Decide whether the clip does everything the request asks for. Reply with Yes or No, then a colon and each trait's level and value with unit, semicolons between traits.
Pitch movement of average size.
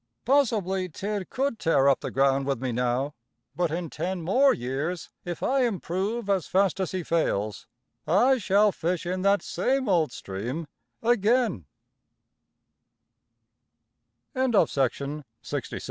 No: wide, 6.1 semitones